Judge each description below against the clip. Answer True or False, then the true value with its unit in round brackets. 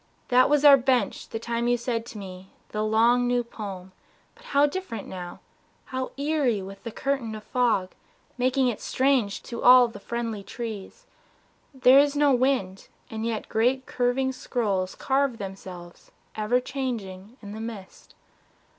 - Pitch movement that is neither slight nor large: True (3.7 semitones)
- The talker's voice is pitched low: False (235 Hz)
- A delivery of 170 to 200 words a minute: False (160 wpm)